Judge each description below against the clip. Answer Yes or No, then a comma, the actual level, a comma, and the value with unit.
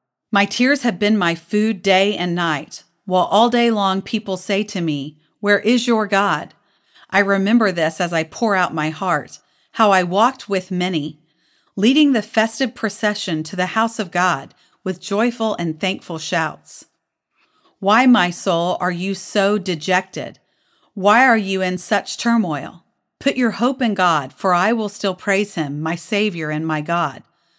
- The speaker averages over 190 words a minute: No, average, 170 wpm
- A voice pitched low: No, high, 195 Hz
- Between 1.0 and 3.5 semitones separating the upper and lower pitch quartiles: No, average, 4.1 semitones